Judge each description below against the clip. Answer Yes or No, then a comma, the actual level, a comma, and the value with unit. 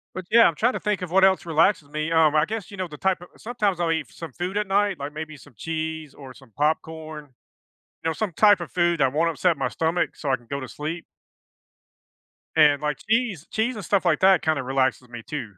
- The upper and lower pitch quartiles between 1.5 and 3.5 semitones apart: No, average, 4.3 semitones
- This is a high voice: No, medium, 160 Hz